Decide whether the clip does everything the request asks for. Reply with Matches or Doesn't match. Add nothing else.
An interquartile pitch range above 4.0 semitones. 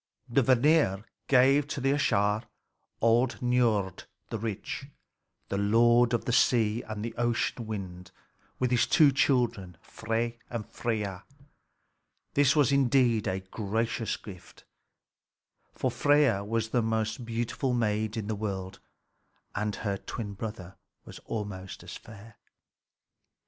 Doesn't match